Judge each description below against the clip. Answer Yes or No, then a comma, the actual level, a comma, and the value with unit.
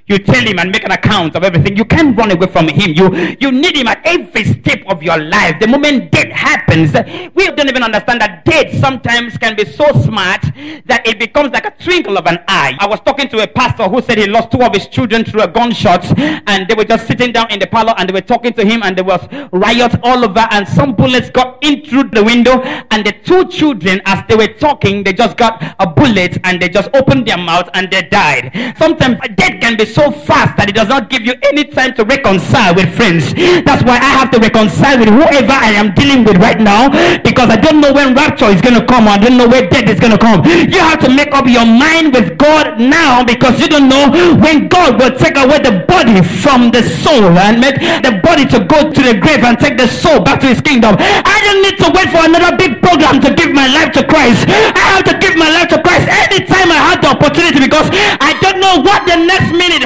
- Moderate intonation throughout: No, wide, 6.0 semitones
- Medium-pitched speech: No, high, 240 Hz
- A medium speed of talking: No, fast, 250 wpm